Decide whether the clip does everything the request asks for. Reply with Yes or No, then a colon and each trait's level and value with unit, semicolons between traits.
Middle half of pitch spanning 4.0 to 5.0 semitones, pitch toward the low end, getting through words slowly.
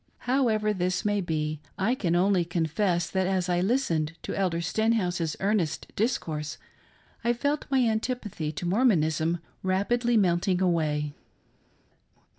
No: average, 4.7 semitones; medium, 185 Hz; slow, 130 wpm